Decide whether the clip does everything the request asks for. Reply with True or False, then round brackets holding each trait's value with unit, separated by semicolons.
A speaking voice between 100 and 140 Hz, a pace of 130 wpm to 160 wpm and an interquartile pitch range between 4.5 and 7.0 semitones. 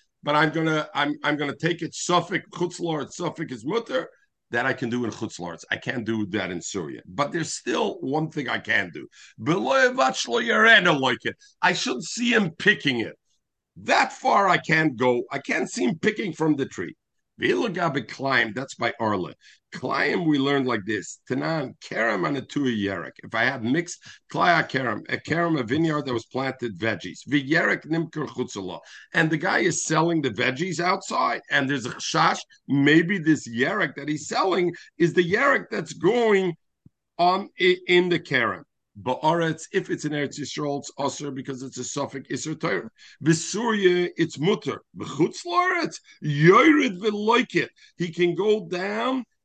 False (160 Hz; 155 wpm; 5.1 semitones)